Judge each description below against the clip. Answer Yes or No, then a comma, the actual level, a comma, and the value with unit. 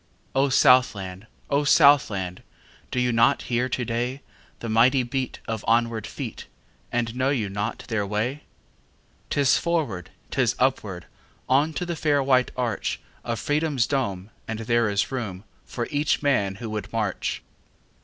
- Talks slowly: Yes, slow, 125 wpm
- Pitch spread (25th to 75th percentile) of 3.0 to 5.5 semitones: Yes, average, 3.8 semitones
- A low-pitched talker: Yes, low, 120 Hz